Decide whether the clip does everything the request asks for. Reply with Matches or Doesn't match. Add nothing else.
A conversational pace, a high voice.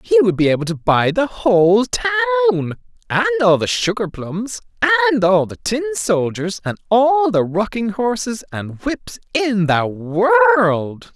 Matches